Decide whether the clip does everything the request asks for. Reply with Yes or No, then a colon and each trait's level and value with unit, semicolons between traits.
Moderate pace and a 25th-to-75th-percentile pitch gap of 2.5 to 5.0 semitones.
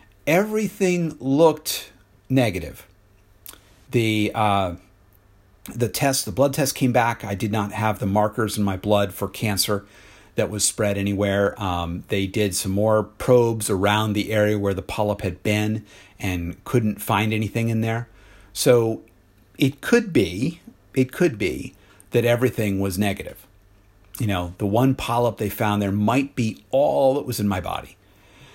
Yes: average, 155 wpm; average, 3.1 semitones